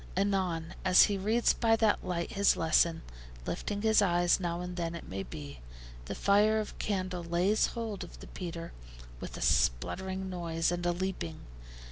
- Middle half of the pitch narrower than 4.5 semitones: Yes, average, 3.1 semitones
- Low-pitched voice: No, medium, 180 Hz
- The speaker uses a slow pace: No, average, 170 wpm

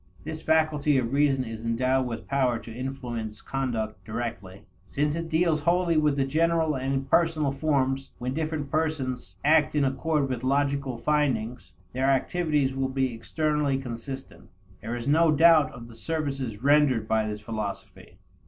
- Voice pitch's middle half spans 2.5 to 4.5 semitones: Yes, average, 4.0 semitones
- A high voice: No, low, 135 Hz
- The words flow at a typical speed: Yes, average, 155 wpm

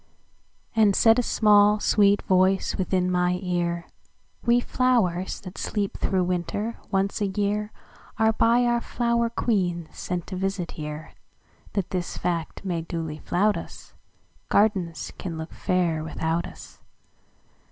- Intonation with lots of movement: No, average, 3.4 semitones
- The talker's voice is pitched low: No, high, 190 Hz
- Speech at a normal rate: No, slow, 120 wpm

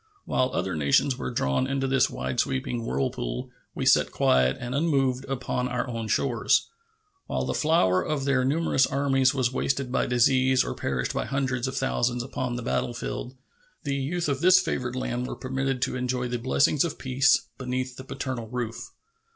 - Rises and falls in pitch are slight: Yes, narrow, 1.9 semitones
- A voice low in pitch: Yes, low, 130 Hz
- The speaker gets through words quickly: No, average, 175 wpm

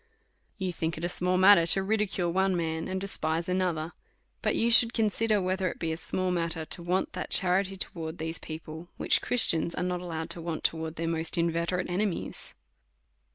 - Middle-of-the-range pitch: Yes, medium, 175 Hz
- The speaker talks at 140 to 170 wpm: No, average, 195 wpm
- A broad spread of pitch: No, narrow, 2.4 semitones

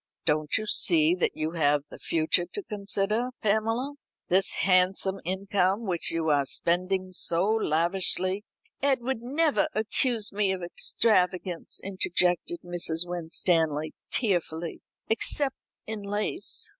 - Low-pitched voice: No, high, 190 Hz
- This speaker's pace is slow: Yes, slow, 120 wpm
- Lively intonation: No, average, 4.3 semitones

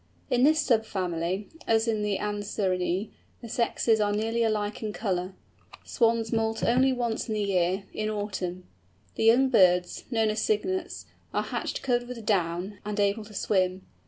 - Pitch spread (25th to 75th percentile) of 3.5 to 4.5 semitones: No, average, 3.0 semitones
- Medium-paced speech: Yes, average, 160 wpm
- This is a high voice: Yes, high, 215 Hz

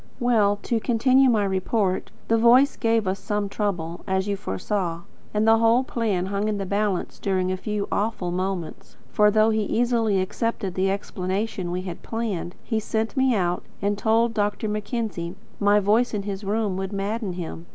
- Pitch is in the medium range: No, high, 205 Hz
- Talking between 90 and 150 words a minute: No, average, 180 wpm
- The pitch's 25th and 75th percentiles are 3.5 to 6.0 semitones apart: No, average, 2.9 semitones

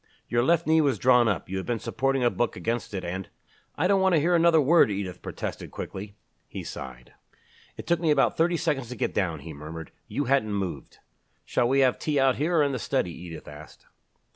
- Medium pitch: No, low, 125 Hz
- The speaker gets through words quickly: Yes, fast, 225 wpm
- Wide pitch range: Yes, wide, 8.0 semitones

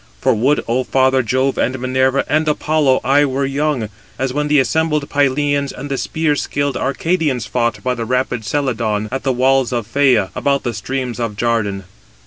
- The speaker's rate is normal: Yes, average, 180 wpm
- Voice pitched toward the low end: Yes, low, 130 Hz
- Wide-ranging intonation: No, average, 2.8 semitones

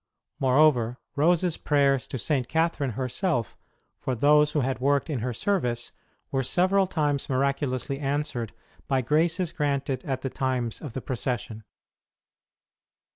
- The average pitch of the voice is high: No, medium, 140 Hz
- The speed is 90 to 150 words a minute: Yes, slow, 135 wpm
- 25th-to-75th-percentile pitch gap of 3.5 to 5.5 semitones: No, average, 3.0 semitones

